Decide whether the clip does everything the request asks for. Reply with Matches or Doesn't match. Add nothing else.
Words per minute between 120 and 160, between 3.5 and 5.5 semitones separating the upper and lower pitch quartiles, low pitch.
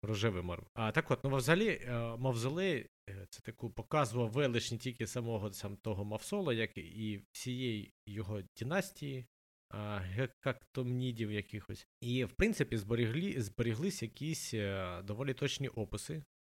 Matches